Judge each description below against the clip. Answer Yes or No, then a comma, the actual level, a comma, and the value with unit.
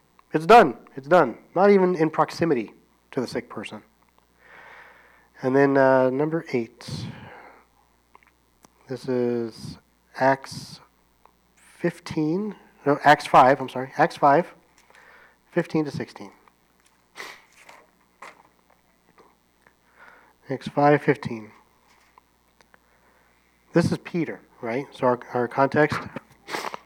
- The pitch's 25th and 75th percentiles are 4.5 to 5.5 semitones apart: Yes, average, 4.9 semitones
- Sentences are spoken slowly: Yes, slow, 95 wpm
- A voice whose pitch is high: No, medium, 140 Hz